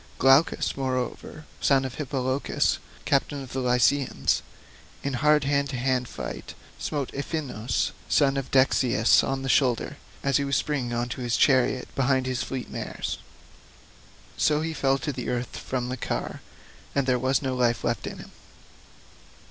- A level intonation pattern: Yes, narrow, 1.9 semitones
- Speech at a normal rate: Yes, average, 155 wpm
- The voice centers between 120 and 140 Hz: Yes, low, 135 Hz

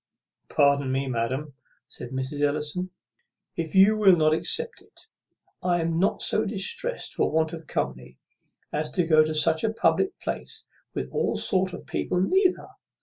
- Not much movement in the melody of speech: No, average, 4.6 semitones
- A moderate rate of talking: Yes, average, 165 wpm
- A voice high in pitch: No, medium, 160 Hz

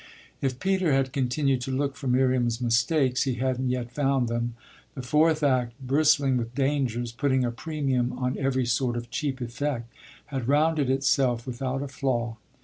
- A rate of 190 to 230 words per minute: No, average, 165 wpm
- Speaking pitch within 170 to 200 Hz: No, low, 130 Hz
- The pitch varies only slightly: Yes, narrow, 2.3 semitones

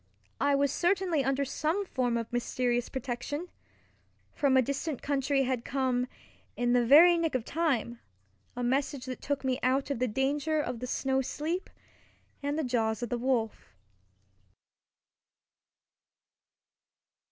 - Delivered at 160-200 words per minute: No, average, 140 wpm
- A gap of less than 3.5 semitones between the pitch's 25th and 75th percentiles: Yes, average, 2.8 semitones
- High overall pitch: Yes, very high, 265 Hz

